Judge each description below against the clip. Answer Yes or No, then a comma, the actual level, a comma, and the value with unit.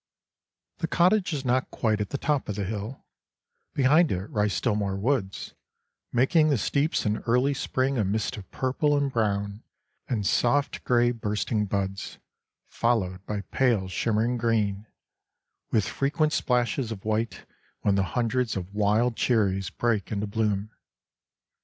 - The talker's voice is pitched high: No, low, 110 Hz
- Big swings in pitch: No, average, 4.2 semitones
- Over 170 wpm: No, average, 145 wpm